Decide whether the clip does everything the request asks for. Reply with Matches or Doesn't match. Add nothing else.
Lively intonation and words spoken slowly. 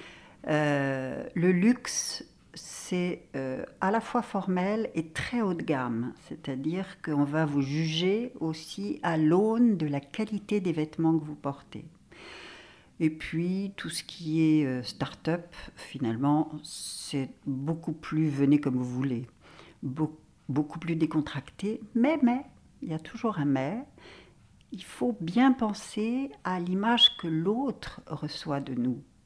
Matches